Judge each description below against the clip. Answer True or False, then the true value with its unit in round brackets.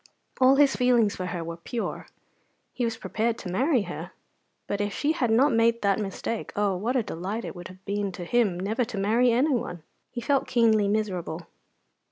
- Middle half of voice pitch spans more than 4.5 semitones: False (3.8 semitones)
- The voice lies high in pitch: True (220 Hz)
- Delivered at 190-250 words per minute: True (195 wpm)